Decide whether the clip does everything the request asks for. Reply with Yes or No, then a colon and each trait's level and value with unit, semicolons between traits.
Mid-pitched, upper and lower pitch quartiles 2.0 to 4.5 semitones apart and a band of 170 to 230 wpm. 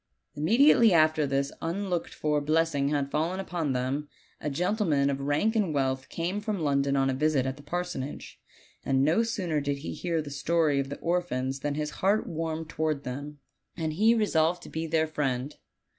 Yes: medium, 155 Hz; average, 3.7 semitones; average, 185 wpm